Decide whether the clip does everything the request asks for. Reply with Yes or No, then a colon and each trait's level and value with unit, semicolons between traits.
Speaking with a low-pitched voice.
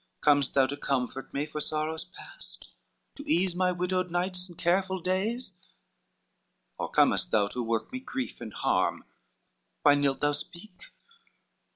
No: medium, 170 Hz